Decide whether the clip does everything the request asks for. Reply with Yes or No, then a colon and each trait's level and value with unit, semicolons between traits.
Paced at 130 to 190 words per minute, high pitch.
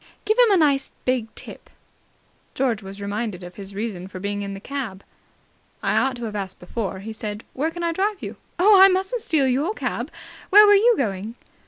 No: fast, 205 wpm; high, 240 Hz